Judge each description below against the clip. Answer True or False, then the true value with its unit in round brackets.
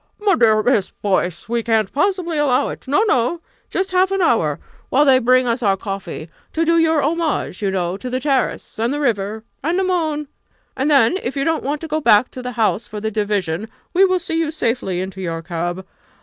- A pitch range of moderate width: False (7.4 semitones)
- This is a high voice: True (250 Hz)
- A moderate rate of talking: False (220 wpm)